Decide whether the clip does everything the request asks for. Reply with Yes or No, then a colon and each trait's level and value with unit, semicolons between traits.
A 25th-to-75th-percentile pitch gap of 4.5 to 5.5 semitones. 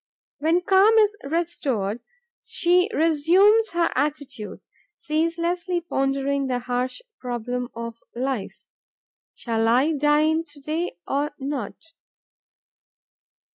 Yes: average, 5.1 semitones